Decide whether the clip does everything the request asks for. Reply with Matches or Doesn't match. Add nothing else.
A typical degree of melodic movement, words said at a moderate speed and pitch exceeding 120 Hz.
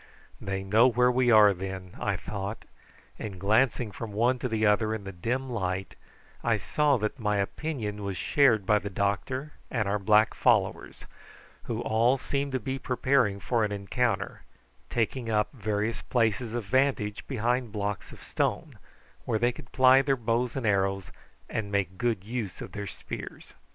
Doesn't match